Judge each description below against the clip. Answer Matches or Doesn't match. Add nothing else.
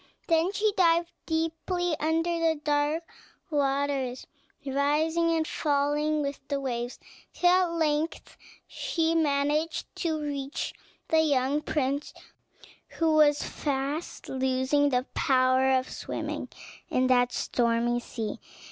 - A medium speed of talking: Doesn't match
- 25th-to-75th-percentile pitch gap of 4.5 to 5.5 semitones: Doesn't match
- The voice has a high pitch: Matches